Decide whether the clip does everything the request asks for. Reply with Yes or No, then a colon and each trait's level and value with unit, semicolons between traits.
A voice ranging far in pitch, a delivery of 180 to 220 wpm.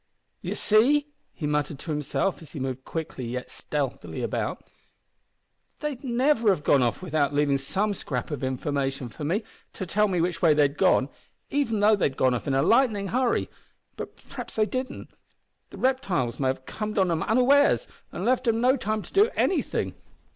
Yes: wide, 8.8 semitones; average, 185 wpm